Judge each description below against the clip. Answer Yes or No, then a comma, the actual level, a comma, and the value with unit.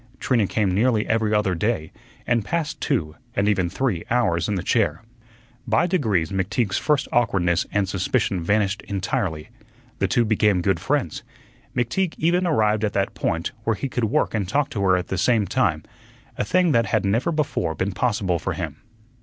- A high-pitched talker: No, low, 105 Hz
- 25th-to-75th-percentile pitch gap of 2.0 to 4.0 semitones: No, average, 4.5 semitones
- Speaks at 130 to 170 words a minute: No, average, 180 wpm